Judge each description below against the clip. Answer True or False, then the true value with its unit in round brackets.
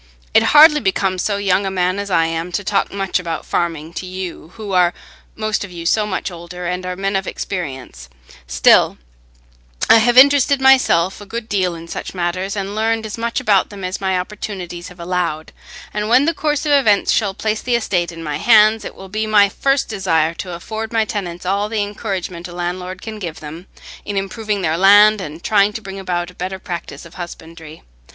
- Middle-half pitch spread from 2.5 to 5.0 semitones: True (3.5 semitones)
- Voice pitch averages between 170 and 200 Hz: True (190 Hz)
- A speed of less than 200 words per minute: False (205 wpm)